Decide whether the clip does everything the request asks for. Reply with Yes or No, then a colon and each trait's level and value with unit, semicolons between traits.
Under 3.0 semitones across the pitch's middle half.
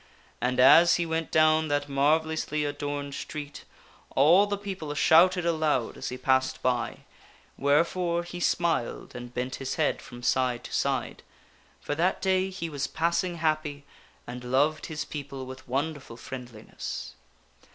No: average, 4.1 semitones